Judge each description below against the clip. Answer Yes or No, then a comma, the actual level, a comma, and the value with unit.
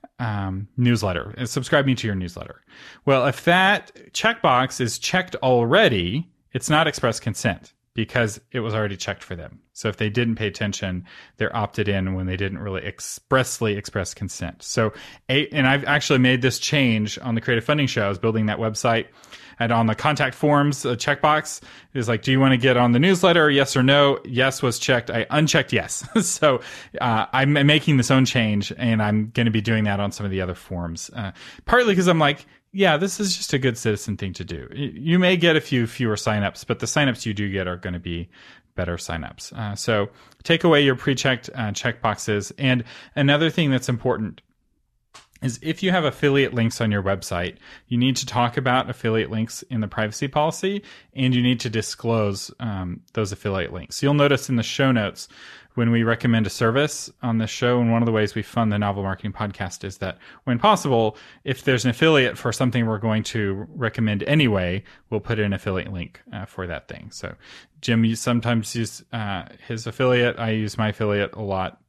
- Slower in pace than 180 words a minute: No, fast, 205 wpm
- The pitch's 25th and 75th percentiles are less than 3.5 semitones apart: No, average, 4.3 semitones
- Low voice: Yes, low, 120 Hz